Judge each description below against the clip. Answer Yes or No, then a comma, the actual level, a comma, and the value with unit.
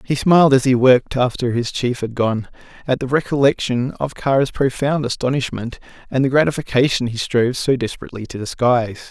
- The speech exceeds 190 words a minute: No, average, 170 wpm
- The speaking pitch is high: No, low, 130 Hz